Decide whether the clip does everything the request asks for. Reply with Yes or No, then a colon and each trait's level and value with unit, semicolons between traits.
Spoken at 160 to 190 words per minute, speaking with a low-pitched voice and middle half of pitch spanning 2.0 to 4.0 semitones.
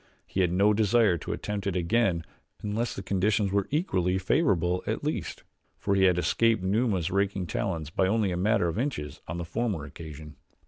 Yes: average, 185 wpm; very low, 95 Hz; average, 3.5 semitones